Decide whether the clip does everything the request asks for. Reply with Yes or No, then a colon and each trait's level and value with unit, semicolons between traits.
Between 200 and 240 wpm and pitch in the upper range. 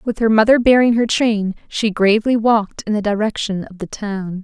Yes: fast, 205 wpm; high, 215 Hz